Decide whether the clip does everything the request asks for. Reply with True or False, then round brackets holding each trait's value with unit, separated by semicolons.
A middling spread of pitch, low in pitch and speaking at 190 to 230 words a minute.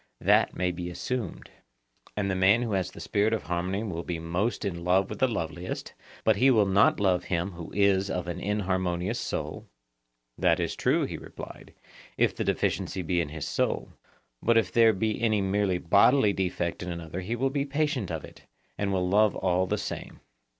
True (3.4 semitones; 95 Hz; 195 wpm)